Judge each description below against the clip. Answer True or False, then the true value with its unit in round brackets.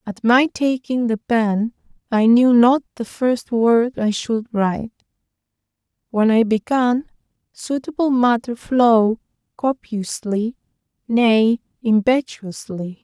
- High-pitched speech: True (235 Hz)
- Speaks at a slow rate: True (105 wpm)